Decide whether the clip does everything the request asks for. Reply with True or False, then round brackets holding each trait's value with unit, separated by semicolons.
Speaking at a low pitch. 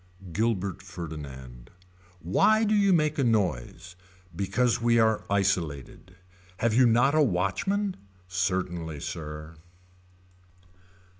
True (95 Hz)